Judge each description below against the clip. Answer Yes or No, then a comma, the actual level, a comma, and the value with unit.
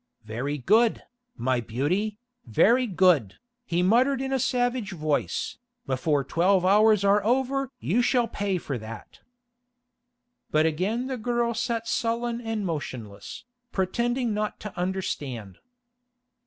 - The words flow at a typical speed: No, slow, 125 wpm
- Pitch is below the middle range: No, high, 200 Hz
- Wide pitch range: Yes, wide, 7.7 semitones